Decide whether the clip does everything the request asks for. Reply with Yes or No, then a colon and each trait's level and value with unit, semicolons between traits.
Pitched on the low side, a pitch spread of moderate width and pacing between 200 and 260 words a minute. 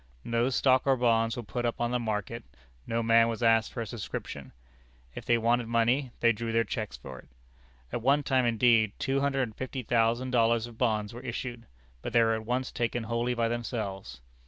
No: low, 115 Hz; narrow, 1.4 semitones; fast, 205 wpm